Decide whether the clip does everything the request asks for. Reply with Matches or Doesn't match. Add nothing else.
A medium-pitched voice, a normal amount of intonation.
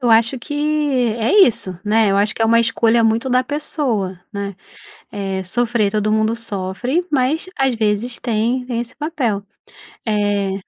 Doesn't match